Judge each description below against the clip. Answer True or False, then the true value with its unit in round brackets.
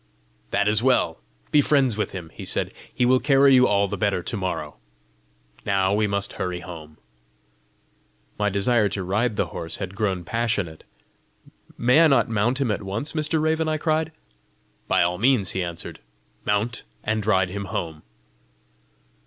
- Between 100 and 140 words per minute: False (165 wpm)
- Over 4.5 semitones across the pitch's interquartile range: True (5.0 semitones)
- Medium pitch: False (105 Hz)